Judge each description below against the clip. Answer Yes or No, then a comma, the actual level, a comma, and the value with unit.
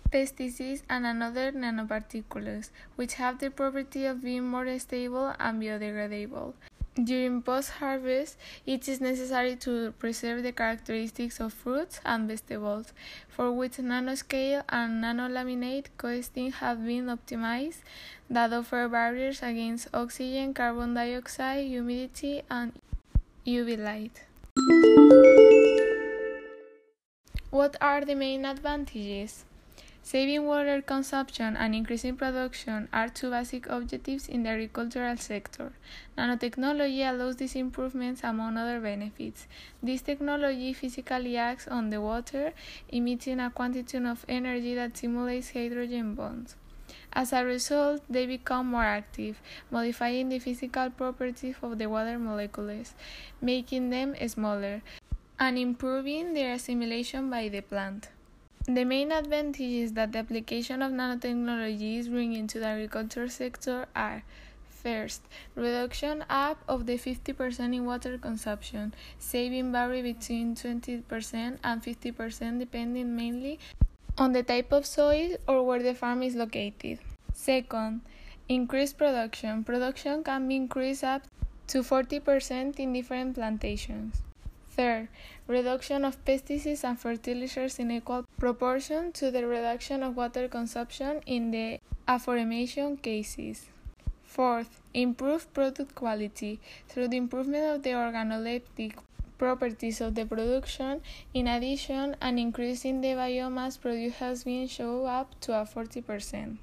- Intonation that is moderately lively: No, narrow, 2.1 semitones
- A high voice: Yes, very high, 250 Hz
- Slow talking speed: Yes, slow, 120 wpm